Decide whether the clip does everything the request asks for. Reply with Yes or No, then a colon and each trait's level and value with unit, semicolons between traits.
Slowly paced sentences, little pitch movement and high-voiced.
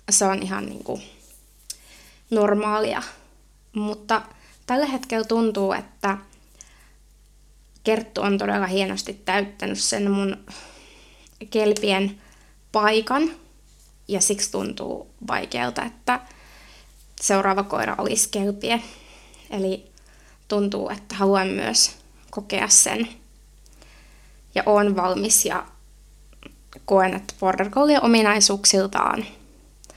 Yes: slow, 90 wpm; narrow, 2.2 semitones; high, 205 Hz